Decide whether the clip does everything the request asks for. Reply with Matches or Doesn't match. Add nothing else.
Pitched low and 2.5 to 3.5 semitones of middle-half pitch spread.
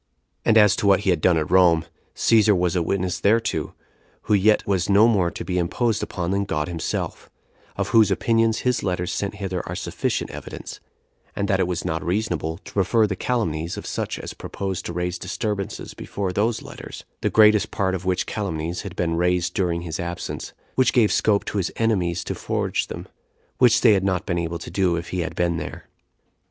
Matches